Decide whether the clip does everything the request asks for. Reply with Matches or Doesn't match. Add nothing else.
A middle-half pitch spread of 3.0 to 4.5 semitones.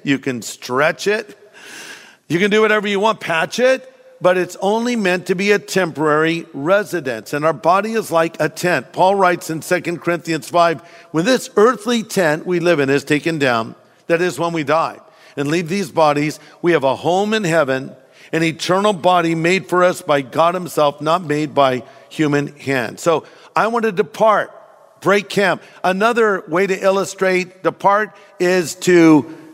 Matches